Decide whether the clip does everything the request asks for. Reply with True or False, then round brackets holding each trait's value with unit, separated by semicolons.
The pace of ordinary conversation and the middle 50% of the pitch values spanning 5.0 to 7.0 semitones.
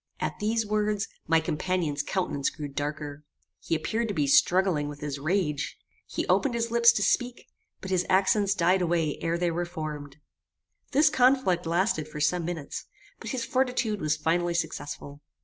True (165 wpm; 5.5 semitones)